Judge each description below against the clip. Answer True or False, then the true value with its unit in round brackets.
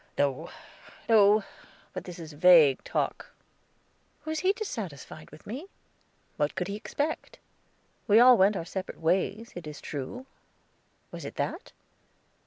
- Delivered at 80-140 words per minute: True (135 wpm)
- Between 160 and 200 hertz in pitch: True (190 Hz)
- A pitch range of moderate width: False (6.6 semitones)